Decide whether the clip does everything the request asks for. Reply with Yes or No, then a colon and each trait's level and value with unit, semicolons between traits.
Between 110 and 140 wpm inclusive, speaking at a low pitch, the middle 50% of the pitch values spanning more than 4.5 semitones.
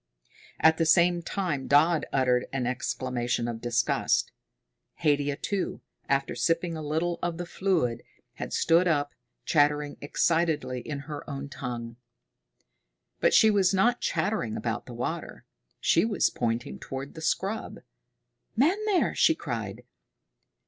No: slow, 135 wpm; medium, 150 Hz; average, 5.0 semitones